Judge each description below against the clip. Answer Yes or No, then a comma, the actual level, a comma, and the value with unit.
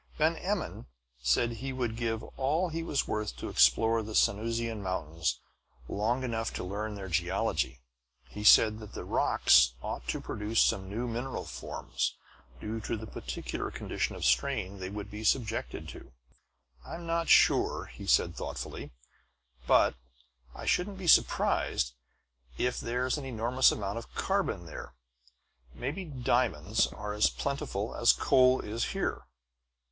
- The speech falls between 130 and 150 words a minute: Yes, average, 145 wpm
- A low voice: Yes, low, 110 Hz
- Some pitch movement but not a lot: Yes, average, 4.5 semitones